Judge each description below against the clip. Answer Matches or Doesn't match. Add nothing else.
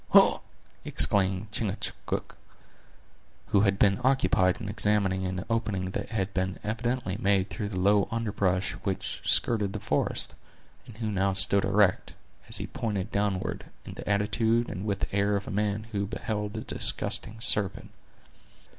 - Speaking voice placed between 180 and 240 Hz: Doesn't match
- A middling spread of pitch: Doesn't match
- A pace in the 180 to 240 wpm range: Doesn't match